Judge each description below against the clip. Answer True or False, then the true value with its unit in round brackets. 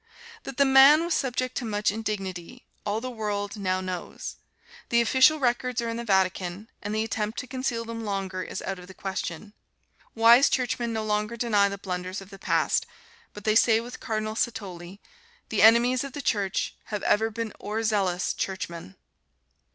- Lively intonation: False (3.4 semitones)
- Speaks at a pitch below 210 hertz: False (215 Hz)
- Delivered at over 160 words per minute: True (180 wpm)